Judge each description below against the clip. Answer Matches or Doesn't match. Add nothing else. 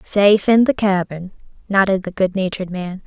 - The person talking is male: Doesn't match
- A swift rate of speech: Doesn't match